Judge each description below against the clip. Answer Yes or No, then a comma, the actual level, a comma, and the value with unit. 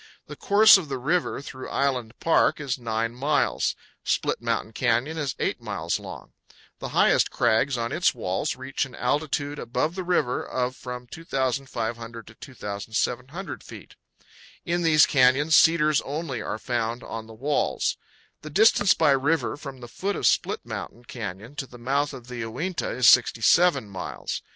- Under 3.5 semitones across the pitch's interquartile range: No, average, 4.3 semitones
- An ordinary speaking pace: Yes, average, 160 wpm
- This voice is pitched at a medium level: No, low, 130 Hz